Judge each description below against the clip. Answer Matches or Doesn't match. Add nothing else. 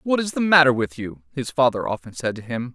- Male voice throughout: Matches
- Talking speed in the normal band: Doesn't match